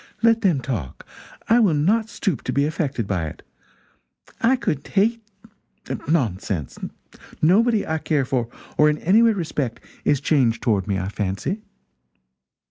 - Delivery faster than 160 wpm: No, average, 145 wpm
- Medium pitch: Yes, medium, 150 Hz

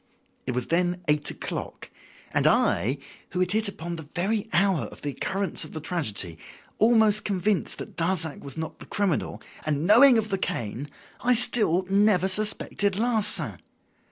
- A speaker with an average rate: Yes, average, 160 wpm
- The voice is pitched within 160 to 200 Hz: Yes, medium, 185 Hz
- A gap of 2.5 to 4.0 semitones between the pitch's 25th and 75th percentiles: No, average, 5.2 semitones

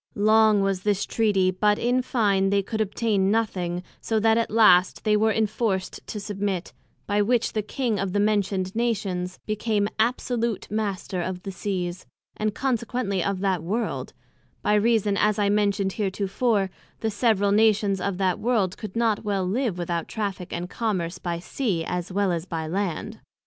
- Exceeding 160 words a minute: Yes, average, 170 wpm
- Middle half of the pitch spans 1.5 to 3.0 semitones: Yes, average, 2.7 semitones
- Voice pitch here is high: Yes, high, 205 Hz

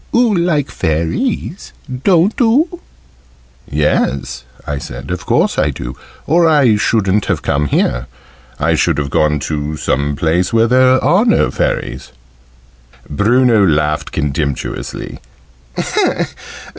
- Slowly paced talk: Yes, slow, 120 wpm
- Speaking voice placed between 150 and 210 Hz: No, very low, 90 Hz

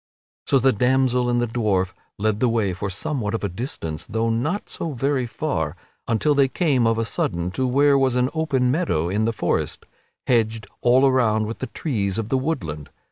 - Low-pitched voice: Yes, low, 120 Hz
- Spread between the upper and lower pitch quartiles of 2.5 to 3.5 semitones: No, average, 3.9 semitones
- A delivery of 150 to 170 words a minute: No, average, 200 wpm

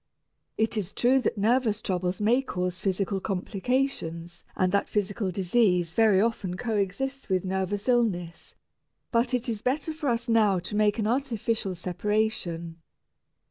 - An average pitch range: Yes, average, 4.1 semitones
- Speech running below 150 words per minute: Yes, average, 140 wpm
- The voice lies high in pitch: Yes, high, 205 Hz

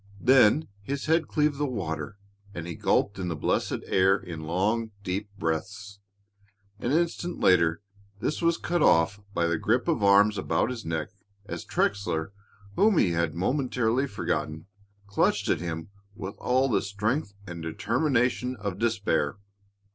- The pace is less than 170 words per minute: Yes, average, 150 wpm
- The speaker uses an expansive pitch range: Yes, wide, 6.6 semitones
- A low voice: Yes, low, 100 Hz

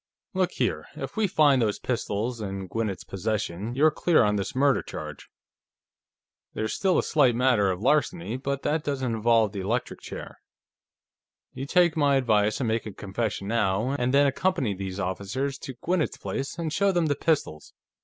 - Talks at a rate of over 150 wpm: Yes, average, 175 wpm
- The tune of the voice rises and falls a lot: Yes, wide, 5.7 semitones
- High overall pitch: No, low, 125 Hz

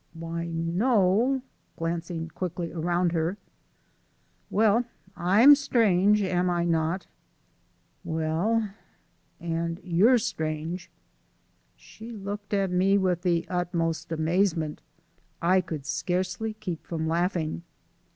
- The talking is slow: Yes, slow, 105 wpm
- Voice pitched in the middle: Yes, medium, 175 Hz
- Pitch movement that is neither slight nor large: Yes, average, 3.3 semitones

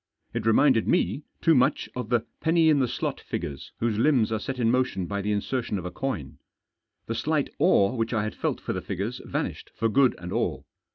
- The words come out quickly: Yes, fast, 215 wpm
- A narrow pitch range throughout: No, average, 3.9 semitones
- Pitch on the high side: No, low, 115 Hz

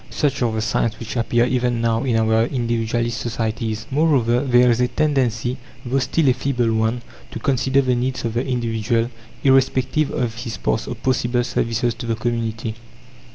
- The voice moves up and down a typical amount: No, narrow, 2.1 semitones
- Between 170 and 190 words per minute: Yes, average, 175 wpm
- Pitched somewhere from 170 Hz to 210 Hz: No, low, 120 Hz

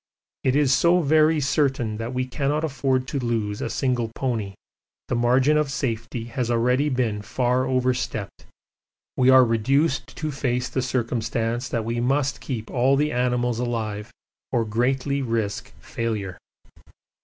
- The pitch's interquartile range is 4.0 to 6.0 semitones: No, narrow, 2.6 semitones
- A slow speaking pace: No, average, 145 wpm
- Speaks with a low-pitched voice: Yes, low, 125 Hz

